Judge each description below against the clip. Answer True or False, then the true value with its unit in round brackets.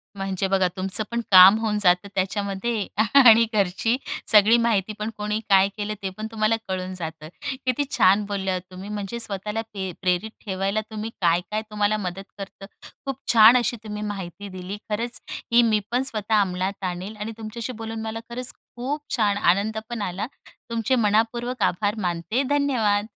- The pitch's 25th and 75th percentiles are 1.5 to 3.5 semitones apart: True (2.8 semitones)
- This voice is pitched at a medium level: False (210 Hz)